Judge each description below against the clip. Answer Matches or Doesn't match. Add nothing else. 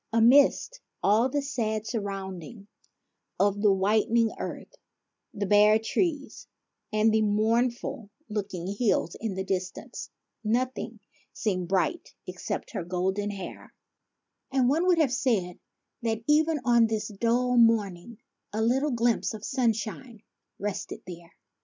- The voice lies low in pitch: Doesn't match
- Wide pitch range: Doesn't match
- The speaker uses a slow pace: Matches